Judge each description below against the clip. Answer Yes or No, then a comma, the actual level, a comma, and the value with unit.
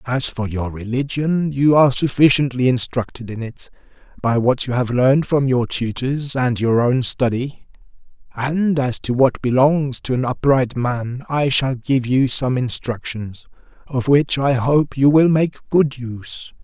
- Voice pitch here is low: Yes, low, 130 Hz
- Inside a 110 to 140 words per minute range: No, average, 165 wpm